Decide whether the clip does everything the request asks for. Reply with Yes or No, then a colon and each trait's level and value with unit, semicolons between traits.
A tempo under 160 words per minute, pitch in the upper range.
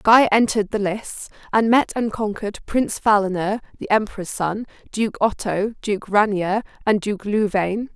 Yes: average, 150 wpm; high, 210 Hz